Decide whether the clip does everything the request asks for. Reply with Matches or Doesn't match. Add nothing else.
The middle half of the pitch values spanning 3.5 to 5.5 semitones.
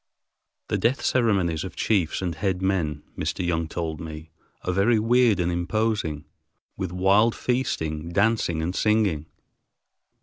Matches